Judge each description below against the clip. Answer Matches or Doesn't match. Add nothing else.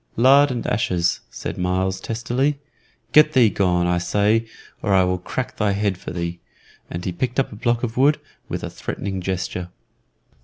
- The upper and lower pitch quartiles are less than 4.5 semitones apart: Doesn't match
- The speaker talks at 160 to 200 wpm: Matches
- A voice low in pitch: Matches